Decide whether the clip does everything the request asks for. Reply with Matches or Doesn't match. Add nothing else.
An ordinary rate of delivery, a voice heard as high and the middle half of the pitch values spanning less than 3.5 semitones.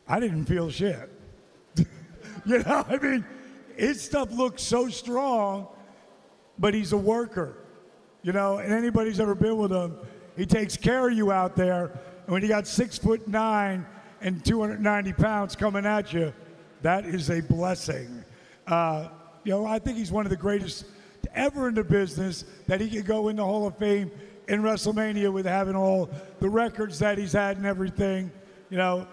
Matches